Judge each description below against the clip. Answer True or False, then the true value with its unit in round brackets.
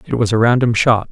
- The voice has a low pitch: True (115 Hz)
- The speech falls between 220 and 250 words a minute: False (270 wpm)